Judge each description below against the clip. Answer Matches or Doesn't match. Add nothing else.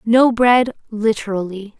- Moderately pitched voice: Doesn't match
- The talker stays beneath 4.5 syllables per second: Matches